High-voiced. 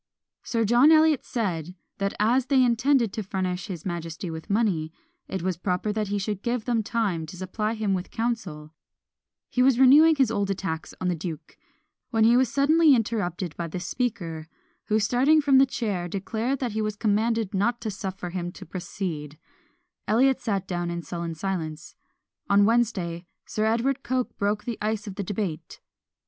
Yes: high, 205 Hz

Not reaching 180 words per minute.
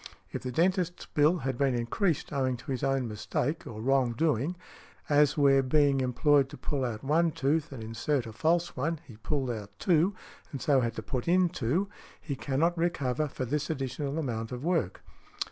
No: average, 185 wpm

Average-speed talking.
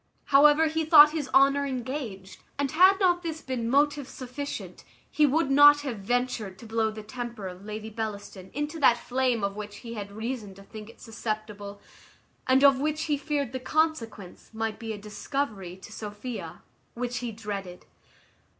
Yes: average, 170 wpm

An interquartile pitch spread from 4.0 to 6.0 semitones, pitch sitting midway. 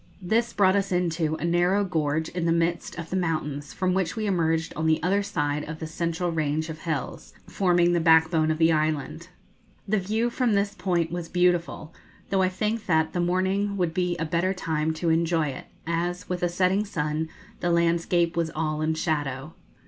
No: narrow, 2.4 semitones; medium, 170 Hz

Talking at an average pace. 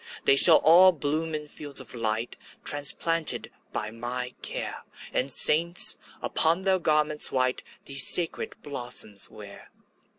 No: slow, 130 wpm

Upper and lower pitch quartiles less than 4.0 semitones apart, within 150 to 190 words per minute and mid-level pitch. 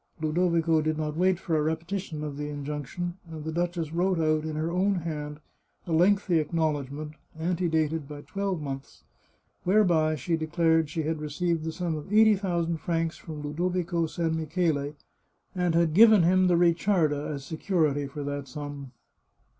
Yes: narrow, 2.6 semitones; average, 175 wpm; medium, 160 Hz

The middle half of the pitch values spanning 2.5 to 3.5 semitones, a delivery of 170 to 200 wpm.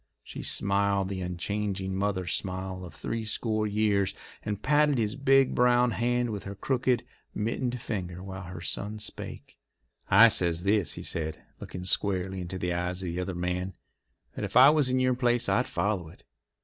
No: average, 4.5 semitones; average, 175 wpm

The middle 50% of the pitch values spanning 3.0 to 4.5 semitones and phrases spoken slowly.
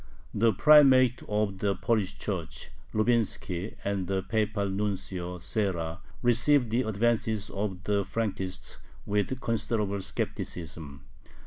Yes: average, 3.3 semitones; slow, 110 wpm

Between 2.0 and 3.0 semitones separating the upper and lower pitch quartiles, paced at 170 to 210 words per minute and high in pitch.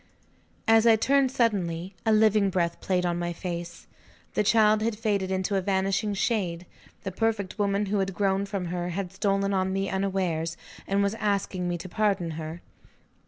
Yes: average, 2.7 semitones; average, 175 wpm; high, 195 Hz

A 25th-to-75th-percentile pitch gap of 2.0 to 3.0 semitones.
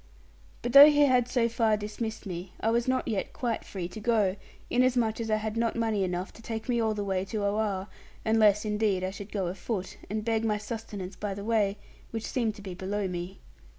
Yes: narrow, 2.6 semitones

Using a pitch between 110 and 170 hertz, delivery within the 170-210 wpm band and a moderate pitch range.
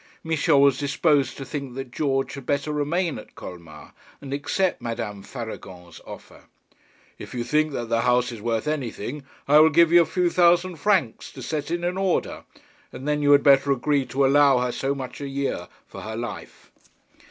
Yes: medium, 140 Hz; average, 190 wpm; average, 3.8 semitones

